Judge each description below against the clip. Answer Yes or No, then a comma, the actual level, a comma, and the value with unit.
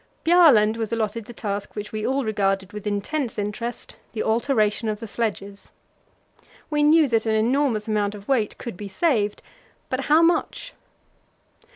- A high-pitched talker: Yes, high, 220 Hz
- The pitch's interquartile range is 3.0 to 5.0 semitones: Yes, average, 4.2 semitones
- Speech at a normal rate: Yes, average, 160 wpm